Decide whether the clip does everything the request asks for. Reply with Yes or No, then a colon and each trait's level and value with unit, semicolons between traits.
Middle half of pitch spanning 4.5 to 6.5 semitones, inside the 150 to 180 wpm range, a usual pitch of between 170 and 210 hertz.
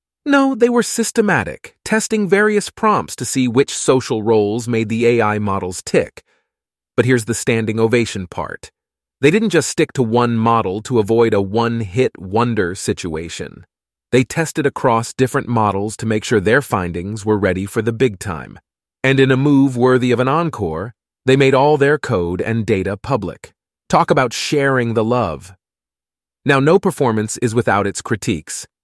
No: average, 5.0 semitones; average, 170 wpm; low, 115 Hz